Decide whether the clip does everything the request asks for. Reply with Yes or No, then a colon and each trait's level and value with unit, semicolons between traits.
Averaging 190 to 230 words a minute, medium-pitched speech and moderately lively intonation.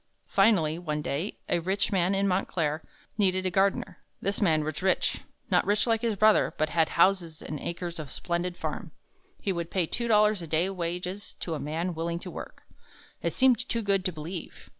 Yes: average, 195 wpm; medium, 180 Hz; average, 3.4 semitones